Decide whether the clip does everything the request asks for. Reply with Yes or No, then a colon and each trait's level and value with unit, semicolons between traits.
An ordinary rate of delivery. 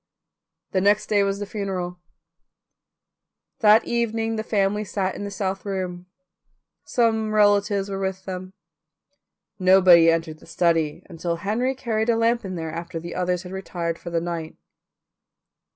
Yes: average, 150 wpm